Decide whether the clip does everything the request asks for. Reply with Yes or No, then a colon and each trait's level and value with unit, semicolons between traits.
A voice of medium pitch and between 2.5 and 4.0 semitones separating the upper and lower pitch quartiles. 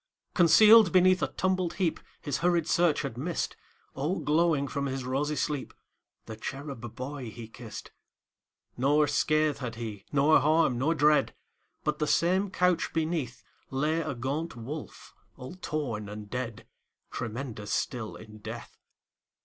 No: medium, 145 Hz; average, 5.1 semitones